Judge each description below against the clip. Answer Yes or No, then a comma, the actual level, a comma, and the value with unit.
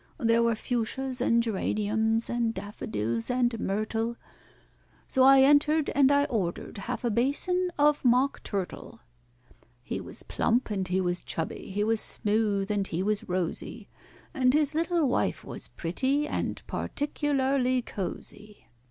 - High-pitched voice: Yes, high, 230 Hz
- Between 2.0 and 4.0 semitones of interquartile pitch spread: No, average, 4.6 semitones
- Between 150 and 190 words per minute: No, average, 140 wpm